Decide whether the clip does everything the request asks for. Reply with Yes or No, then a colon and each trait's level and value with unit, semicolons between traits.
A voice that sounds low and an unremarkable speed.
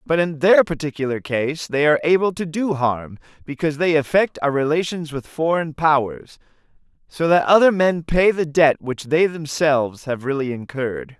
No: medium, 150 Hz; average, 170 wpm